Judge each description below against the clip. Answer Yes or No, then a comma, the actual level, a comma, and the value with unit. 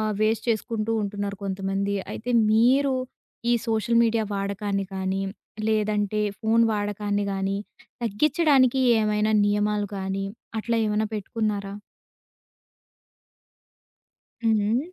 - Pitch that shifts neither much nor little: No, narrow, 1.9 semitones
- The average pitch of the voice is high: Yes, high, 210 Hz